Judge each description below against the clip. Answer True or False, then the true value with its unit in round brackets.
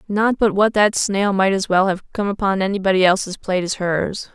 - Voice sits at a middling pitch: False (195 Hz)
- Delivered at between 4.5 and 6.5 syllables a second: True (5.4 syllables/s)